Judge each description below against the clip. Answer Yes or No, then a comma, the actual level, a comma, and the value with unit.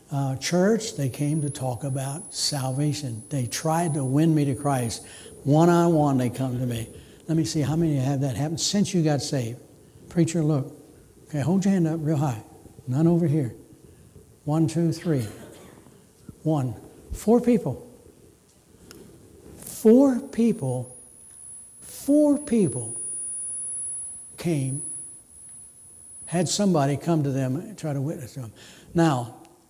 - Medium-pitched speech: Yes, medium, 150 Hz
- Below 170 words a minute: Yes, slow, 135 wpm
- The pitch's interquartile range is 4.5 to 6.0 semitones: No, average, 4.0 semitones